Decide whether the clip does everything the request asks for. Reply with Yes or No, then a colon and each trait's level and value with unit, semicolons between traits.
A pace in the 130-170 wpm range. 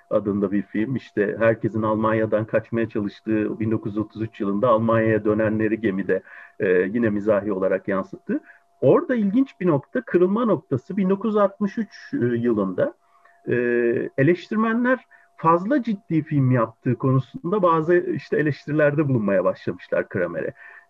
No: average, 105 wpm